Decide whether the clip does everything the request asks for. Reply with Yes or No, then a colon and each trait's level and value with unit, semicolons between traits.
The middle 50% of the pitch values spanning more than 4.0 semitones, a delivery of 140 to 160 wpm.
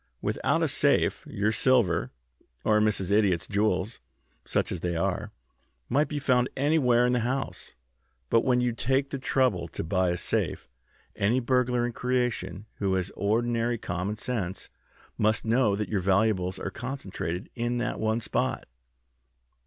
Yes: average, 4.4 semitones; average, 155 wpm